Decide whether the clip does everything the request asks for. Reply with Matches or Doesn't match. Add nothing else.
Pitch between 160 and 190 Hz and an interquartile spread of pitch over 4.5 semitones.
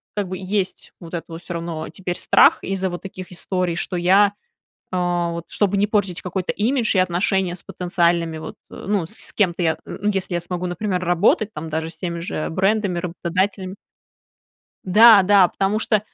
Doesn't match